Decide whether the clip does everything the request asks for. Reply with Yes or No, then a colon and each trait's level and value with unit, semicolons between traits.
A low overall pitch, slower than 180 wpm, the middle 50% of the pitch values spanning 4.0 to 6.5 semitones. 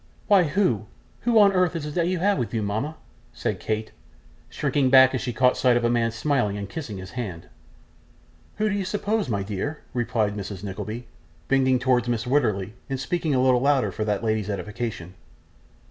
No: low, 125 Hz; average, 190 wpm; wide, 5.6 semitones